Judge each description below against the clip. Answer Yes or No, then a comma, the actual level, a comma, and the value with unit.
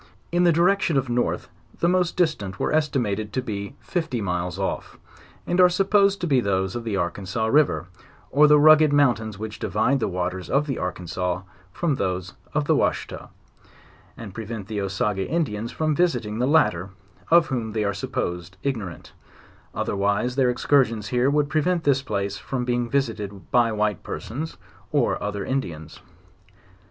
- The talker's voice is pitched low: Yes, low, 115 Hz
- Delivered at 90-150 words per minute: No, average, 170 wpm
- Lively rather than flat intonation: Yes, wide, 6.8 semitones